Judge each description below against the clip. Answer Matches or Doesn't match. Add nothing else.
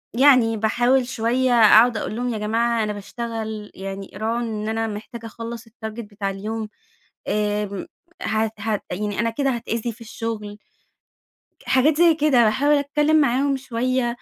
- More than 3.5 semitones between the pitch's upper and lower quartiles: Doesn't match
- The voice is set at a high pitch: Matches